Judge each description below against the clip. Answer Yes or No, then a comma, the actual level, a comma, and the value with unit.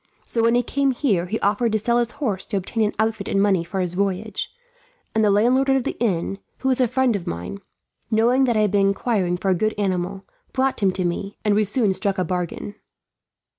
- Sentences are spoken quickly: Yes, fast, 230 wpm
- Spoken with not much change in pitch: No, average, 3.8 semitones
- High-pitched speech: Yes, high, 210 Hz